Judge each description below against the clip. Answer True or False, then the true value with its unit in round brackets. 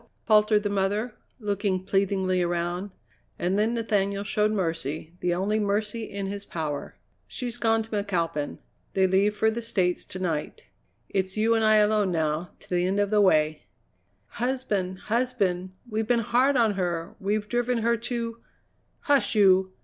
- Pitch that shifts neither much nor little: True (3.1 semitones)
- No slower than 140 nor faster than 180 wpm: True (165 wpm)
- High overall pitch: True (200 Hz)